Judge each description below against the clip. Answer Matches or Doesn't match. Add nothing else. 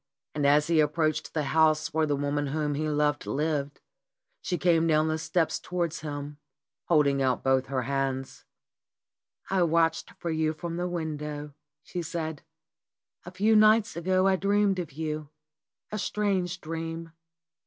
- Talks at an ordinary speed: Matches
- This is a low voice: Doesn't match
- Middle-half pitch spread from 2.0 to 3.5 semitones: Matches